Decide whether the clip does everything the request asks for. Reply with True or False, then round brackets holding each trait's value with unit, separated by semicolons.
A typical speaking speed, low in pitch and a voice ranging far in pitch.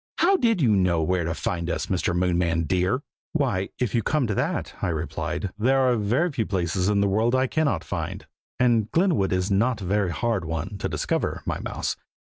False (210 wpm; 100 Hz; 5.7 semitones)